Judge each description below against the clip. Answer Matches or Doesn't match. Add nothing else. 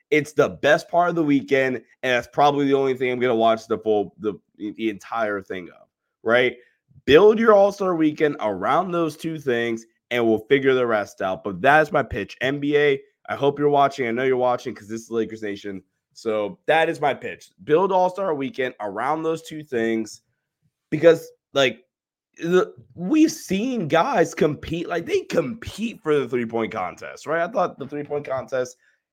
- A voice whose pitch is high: Doesn't match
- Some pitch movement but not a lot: Doesn't match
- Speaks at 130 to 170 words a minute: Doesn't match